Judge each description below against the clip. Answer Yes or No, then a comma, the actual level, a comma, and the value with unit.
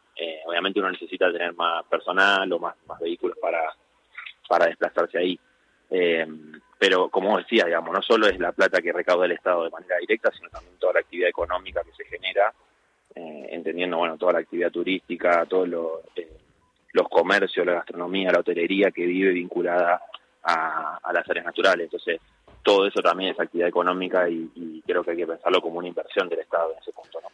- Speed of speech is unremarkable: No, fast, 195 wpm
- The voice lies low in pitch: Yes, very low, 90 Hz